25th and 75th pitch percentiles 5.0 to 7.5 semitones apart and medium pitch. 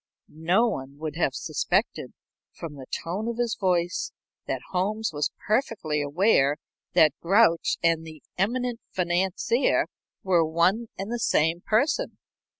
Yes: wide, 5.6 semitones; medium, 180 Hz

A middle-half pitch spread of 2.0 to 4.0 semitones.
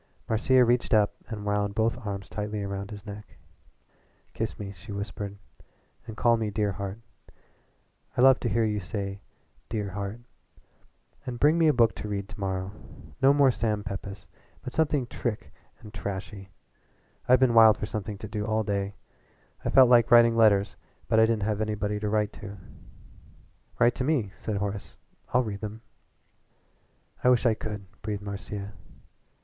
Yes: narrow, 2.5 semitones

